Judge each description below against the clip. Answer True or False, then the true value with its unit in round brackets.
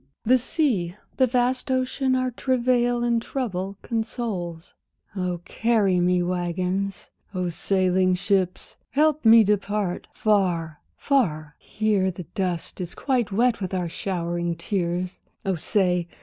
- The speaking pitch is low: False (195 Hz)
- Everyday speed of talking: False (125 wpm)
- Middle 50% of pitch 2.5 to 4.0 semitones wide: False (5.1 semitones)